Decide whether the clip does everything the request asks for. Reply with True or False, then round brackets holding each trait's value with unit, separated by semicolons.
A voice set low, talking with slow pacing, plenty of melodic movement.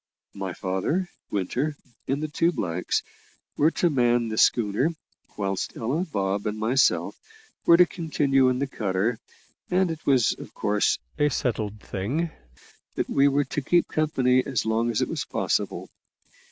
False (125 Hz; 155 wpm; 6.1 semitones)